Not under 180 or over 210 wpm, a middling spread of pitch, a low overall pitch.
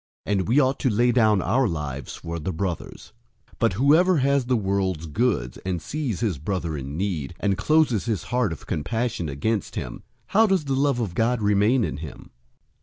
No: average, 190 wpm; wide, 6.9 semitones; low, 105 Hz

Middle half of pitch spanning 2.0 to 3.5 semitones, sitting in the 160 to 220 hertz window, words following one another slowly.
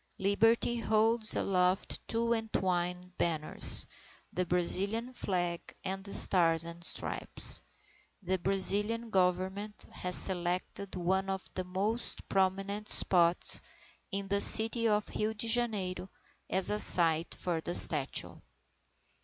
Yes: average, 3.0 semitones; high, 190 Hz; slow, 115 wpm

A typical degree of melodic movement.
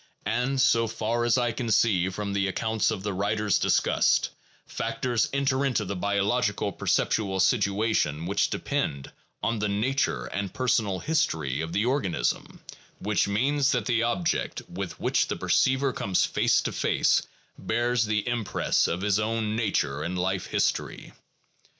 Yes: average, 3.6 semitones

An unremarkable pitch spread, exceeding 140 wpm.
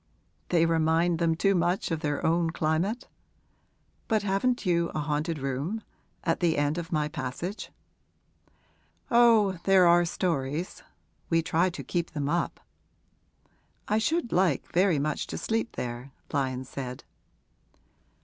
No: average, 3.8 semitones; slow, 135 wpm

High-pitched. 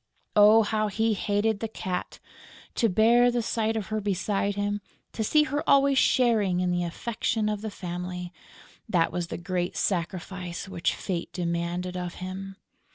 Yes: high, 200 Hz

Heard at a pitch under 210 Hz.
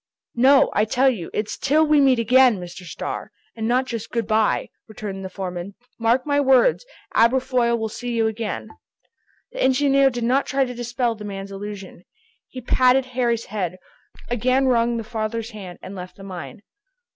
No: high, 230 Hz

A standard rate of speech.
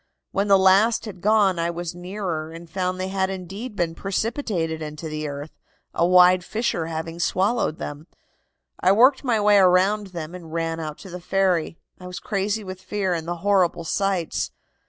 Yes: average, 180 wpm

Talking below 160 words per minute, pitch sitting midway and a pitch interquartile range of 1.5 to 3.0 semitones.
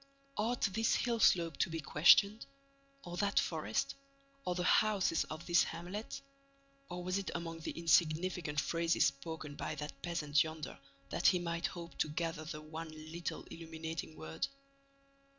Yes: average, 150 wpm; medium, 165 Hz; narrow, 2.4 semitones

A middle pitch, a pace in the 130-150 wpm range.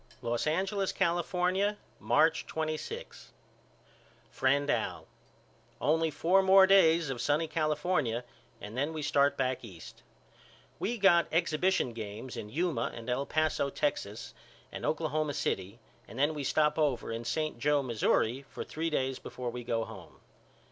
Yes: medium, 150 Hz; average, 140 wpm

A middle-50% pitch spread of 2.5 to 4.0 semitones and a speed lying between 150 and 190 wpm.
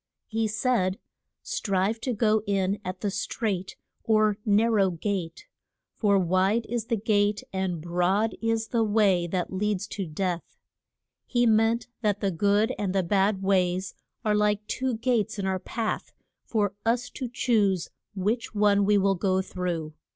Yes: average, 2.8 semitones; average, 160 wpm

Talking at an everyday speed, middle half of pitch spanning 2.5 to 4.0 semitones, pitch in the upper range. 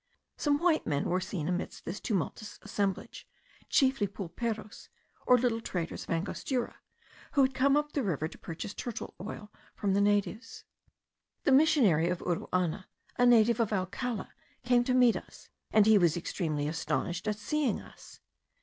No: average, 160 wpm; wide, 5.4 semitones; high, 210 Hz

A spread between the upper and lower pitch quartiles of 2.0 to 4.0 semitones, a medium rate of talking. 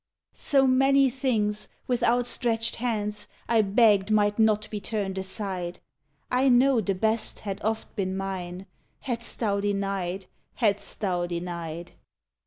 No: average, 3.3 semitones; slow, 130 wpm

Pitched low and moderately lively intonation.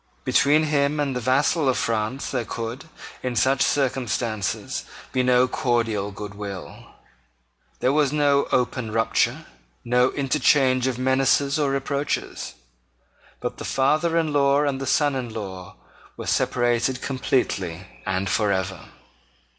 Yes: low, 130 Hz; average, 3.7 semitones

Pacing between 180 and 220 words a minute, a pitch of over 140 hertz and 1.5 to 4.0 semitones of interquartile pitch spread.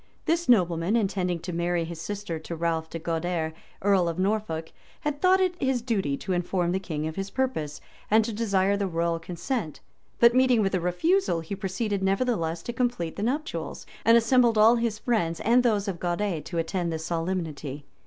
No: average, 190 wpm; high, 190 Hz; wide, 5.5 semitones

